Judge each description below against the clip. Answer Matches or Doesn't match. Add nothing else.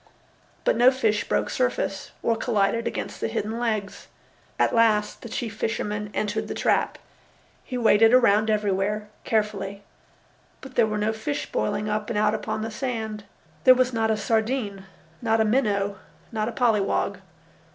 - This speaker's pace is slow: Doesn't match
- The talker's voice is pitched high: Matches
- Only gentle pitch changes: Matches